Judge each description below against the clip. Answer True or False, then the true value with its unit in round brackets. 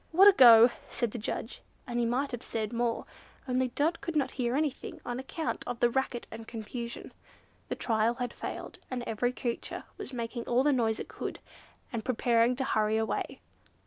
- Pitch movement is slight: True (2.2 semitones)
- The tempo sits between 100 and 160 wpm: False (190 wpm)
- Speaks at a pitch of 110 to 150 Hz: False (240 Hz)